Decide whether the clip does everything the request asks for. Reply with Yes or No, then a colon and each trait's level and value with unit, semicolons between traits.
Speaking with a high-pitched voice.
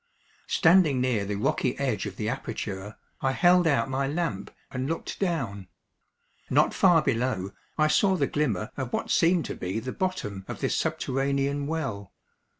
No: low, 135 Hz